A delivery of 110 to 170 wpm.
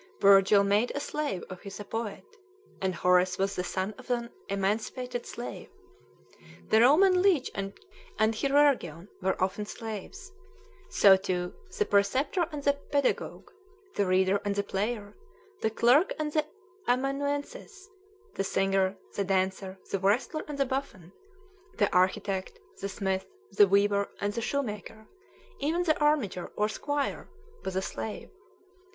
Yes: average, 140 wpm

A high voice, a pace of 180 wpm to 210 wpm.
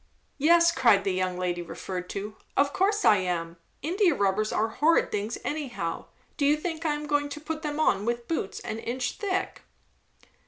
Yes: very high, 255 Hz; average, 185 wpm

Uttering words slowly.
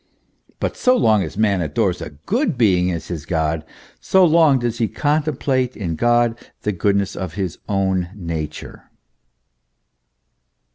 No: average, 145 wpm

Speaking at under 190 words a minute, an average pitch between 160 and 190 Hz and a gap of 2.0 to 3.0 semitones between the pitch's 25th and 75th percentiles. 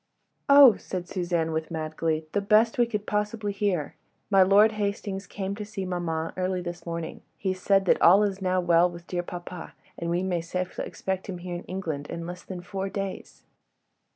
No: average, 195 wpm; medium, 185 Hz; narrow, 2.5 semitones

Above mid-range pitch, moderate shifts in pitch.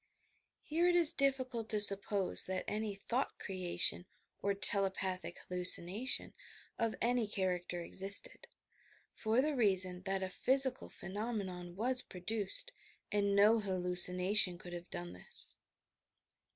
Yes: high, 200 Hz; average, 4.0 semitones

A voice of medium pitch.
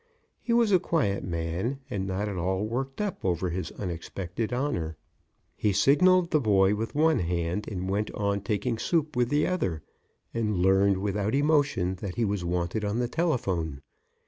No: low, 105 Hz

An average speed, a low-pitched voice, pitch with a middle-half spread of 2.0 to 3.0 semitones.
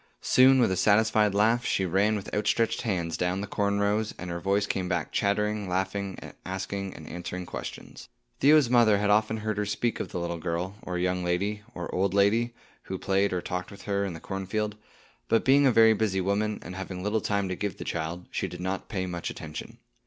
No: fast, 210 wpm; low, 100 Hz; average, 2.7 semitones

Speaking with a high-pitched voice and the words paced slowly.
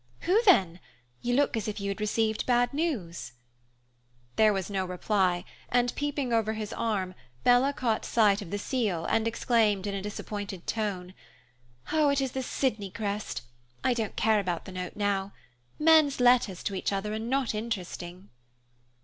No: high, 215 Hz; average, 165 wpm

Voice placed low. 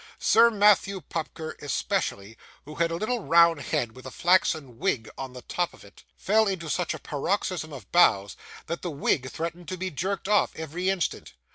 No: medium, 170 Hz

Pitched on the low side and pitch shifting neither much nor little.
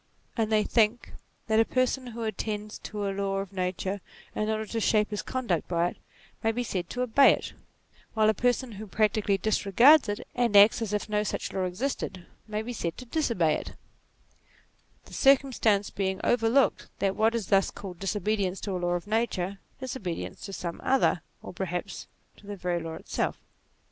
No: high, 210 Hz; average, 3.0 semitones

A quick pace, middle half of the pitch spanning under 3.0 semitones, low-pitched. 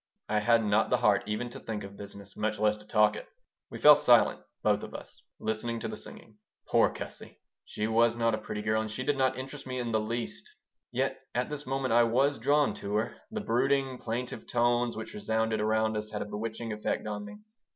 Yes: fast, 220 wpm; narrow, 2.4 semitones; low, 110 Hz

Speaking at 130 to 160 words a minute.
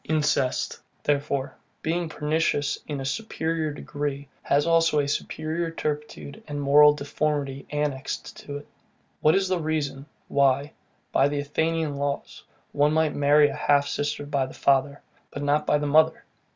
Yes: average, 150 wpm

